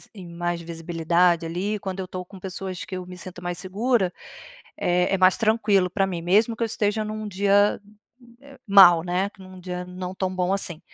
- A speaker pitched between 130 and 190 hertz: Yes, medium, 185 Hz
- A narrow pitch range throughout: Yes, narrow, 2.0 semitones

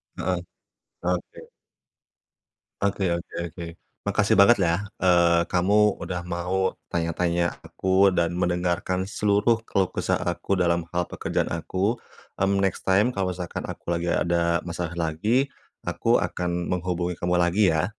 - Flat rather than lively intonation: Yes, narrow, 1.8 semitones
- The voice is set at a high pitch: No, very low, 90 Hz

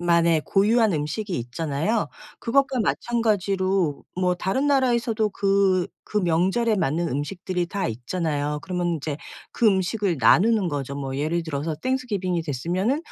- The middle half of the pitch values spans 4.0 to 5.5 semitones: Yes, average, 5.2 semitones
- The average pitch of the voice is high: No, medium, 180 Hz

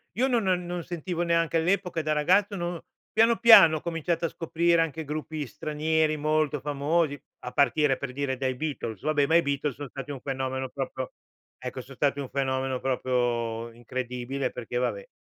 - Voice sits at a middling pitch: Yes, medium, 150 Hz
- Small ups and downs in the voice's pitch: No, average, 4.1 semitones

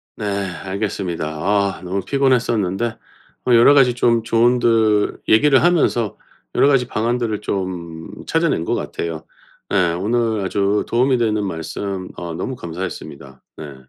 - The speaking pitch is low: Yes, low, 105 Hz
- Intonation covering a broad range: No, average, 4.6 semitones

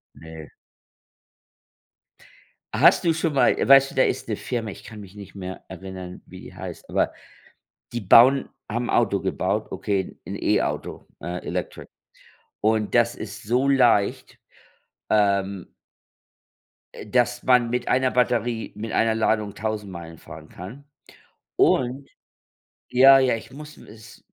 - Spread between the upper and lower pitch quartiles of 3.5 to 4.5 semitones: Yes, average, 4.0 semitones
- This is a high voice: No, low, 110 Hz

